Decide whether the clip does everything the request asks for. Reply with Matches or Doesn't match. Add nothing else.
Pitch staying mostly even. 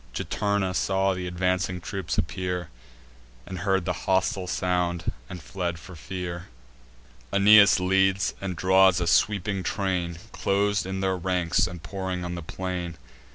Matches